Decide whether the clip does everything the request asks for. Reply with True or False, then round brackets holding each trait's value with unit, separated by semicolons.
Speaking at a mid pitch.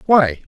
True (150 Hz)